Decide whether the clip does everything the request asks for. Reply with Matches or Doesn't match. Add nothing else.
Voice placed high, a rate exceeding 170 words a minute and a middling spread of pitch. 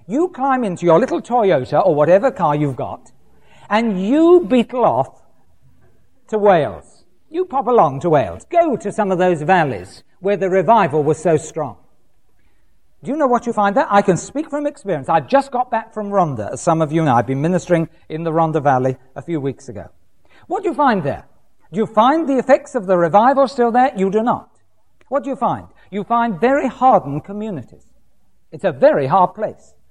Doesn't match